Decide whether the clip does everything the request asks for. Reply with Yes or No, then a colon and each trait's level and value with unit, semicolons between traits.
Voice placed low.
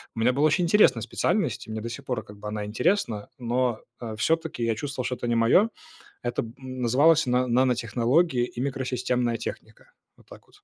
Yes: low, 125 Hz